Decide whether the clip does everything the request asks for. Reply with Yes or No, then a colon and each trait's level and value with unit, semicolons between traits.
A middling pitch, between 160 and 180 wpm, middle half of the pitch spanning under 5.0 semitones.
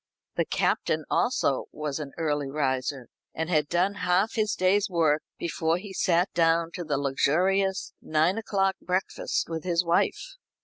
No: medium, 170 Hz; average, 150 wpm; average, 3.9 semitones